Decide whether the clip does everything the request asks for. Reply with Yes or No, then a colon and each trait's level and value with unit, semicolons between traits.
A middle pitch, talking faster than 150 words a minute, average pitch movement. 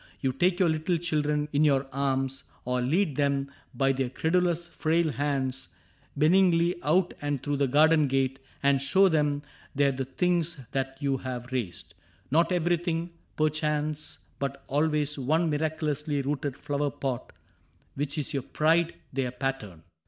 No: medium, 145 Hz; average, 145 wpm; average, 3.0 semitones